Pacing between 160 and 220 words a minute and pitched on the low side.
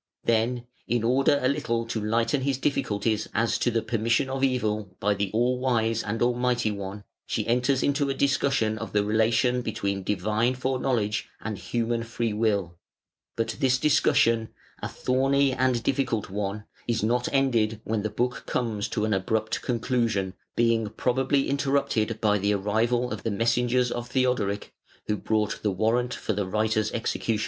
Yes: average, 165 wpm; low, 115 Hz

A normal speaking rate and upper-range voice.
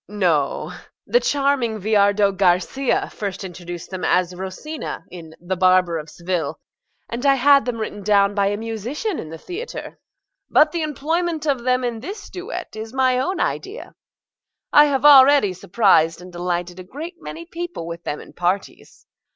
Yes: average, 170 wpm; high, 215 Hz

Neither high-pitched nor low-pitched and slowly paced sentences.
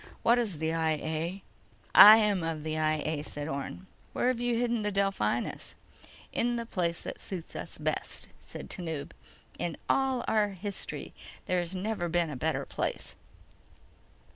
No: medium, 180 Hz; average, 160 wpm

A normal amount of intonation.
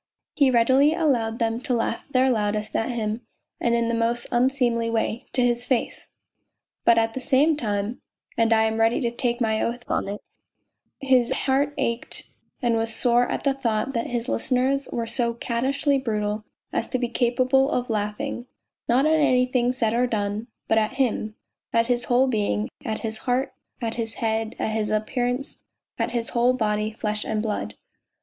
No: narrow, 2.3 semitones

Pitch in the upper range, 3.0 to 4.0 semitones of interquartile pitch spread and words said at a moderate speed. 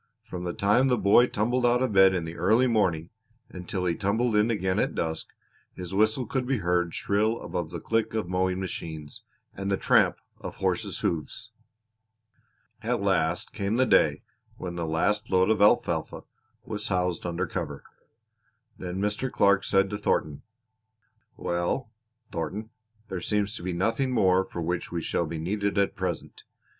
No: very low, 95 Hz; average, 3.7 semitones; average, 170 wpm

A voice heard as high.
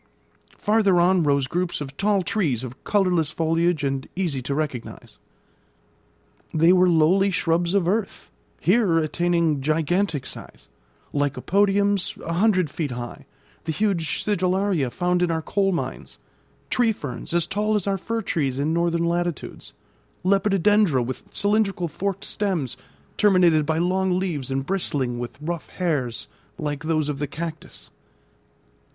No: medium, 170 Hz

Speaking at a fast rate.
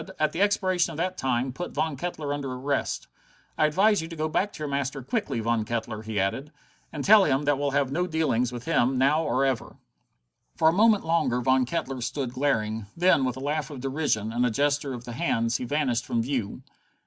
Yes: fast, 225 wpm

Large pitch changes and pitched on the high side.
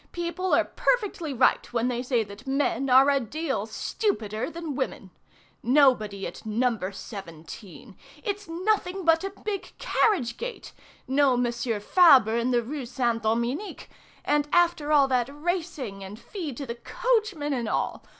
Yes: wide, 6.3 semitones; very high, 270 Hz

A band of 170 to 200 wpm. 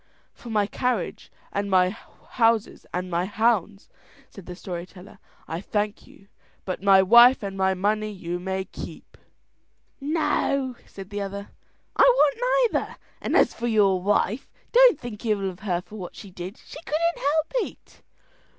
No: average, 160 wpm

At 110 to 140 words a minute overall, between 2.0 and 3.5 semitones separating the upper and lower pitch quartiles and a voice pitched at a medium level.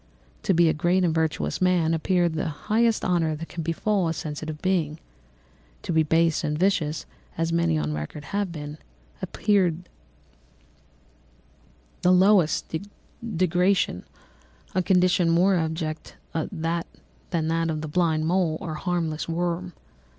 Yes: slow, 135 wpm; narrow, 2.4 semitones; medium, 165 Hz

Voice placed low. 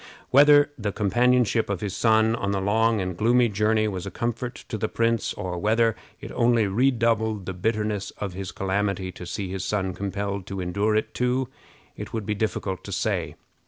Yes: low, 105 Hz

